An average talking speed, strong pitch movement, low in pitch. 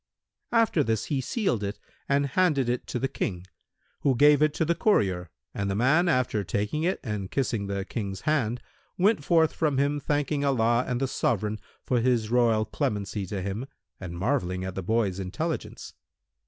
Yes: average, 180 wpm; wide, 6.2 semitones; low, 120 Hz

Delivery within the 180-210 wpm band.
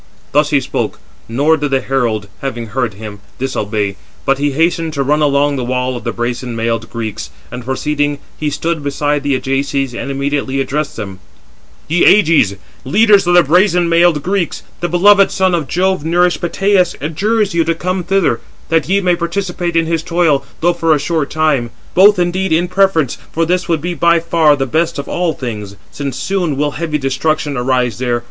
Yes: average, 190 wpm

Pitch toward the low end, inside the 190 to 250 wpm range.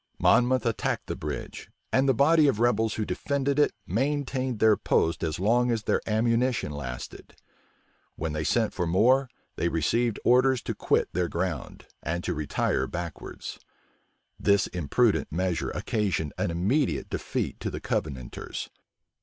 No: low, 110 Hz; average, 145 wpm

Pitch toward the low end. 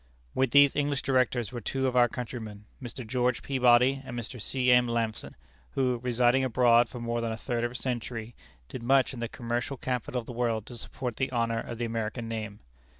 Yes: low, 120 Hz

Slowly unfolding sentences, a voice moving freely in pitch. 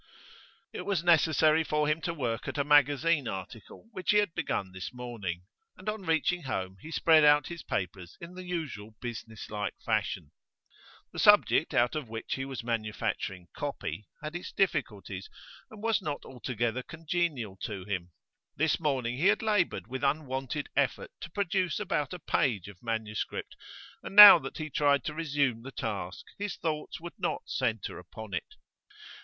No: average, 165 wpm; wide, 6.8 semitones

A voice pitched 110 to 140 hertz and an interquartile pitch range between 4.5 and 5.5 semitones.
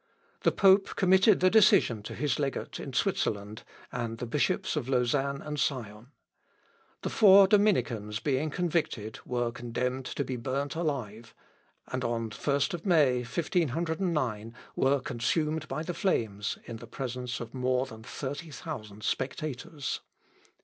Yes: low, 135 Hz; average, 5.2 semitones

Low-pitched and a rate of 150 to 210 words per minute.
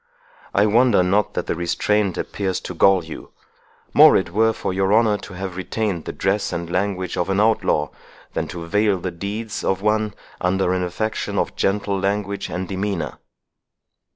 Yes: very low, 95 Hz; average, 170 wpm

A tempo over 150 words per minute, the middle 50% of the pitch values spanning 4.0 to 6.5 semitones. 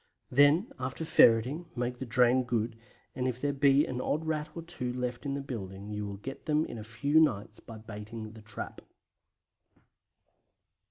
Yes: average, 175 wpm; average, 4.4 semitones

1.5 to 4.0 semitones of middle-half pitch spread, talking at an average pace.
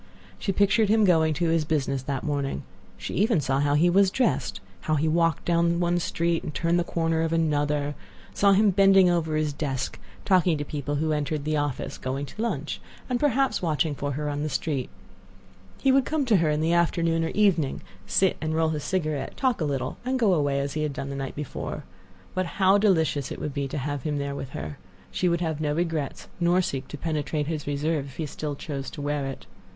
No: average, 3.3 semitones; fast, 225 wpm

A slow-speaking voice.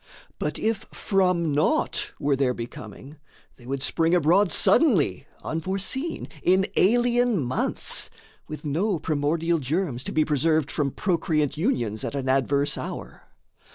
Yes: slow, 130 wpm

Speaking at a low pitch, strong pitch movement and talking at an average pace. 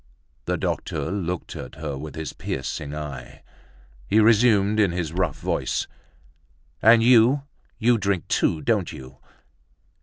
No: very low, 90 Hz; wide, 6.5 semitones; slow, 130 wpm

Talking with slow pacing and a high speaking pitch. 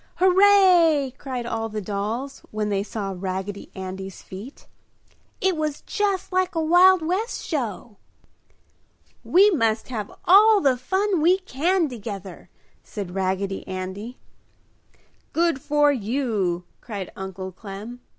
Yes: slow, 125 wpm; high, 245 Hz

